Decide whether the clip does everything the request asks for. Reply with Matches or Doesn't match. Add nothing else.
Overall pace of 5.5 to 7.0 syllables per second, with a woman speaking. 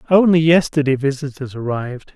Doesn't match